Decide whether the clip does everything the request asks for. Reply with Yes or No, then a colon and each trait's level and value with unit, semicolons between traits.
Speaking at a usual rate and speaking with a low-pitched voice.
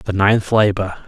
Yes: average, 170 wpm; low, 100 Hz